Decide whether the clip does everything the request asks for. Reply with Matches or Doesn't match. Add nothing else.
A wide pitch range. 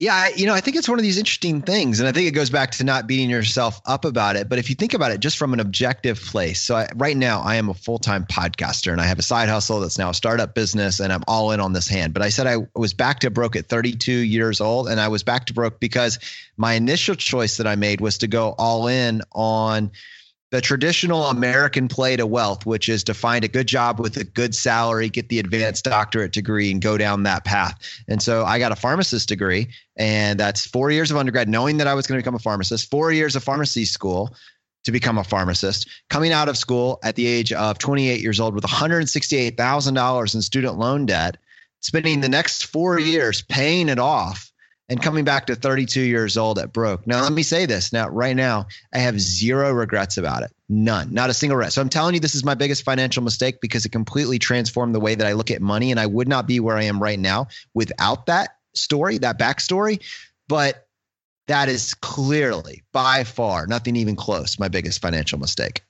Doesn't match